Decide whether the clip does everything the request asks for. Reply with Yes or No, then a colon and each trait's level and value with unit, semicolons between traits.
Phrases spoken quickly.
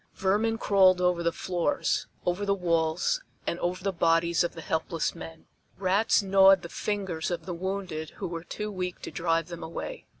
No: average, 180 wpm